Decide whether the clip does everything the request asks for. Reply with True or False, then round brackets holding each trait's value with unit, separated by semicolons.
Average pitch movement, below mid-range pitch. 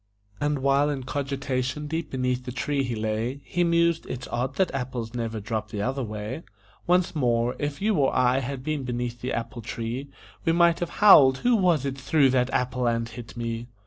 True (3.5 semitones; 130 Hz)